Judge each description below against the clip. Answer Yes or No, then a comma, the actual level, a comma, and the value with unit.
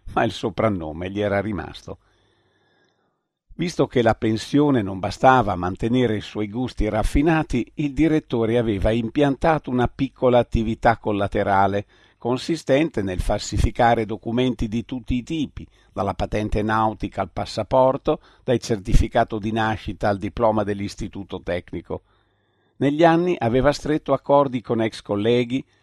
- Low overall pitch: Yes, low, 115 Hz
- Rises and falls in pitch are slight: No, average, 3.9 semitones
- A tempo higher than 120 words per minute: Yes, average, 130 wpm